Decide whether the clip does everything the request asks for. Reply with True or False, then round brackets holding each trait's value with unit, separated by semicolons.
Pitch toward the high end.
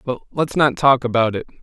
False (125 Hz)